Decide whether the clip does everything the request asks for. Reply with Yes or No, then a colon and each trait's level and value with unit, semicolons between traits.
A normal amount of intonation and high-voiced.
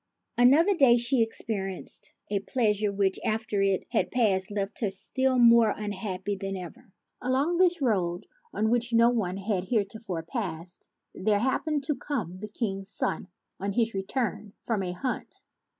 Yes: average, 3.9 semitones; high, 215 Hz